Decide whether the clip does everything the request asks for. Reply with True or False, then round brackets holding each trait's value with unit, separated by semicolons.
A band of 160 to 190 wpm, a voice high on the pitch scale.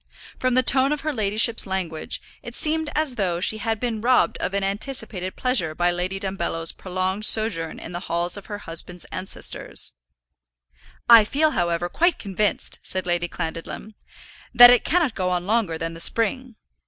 True (170 wpm; 200 Hz)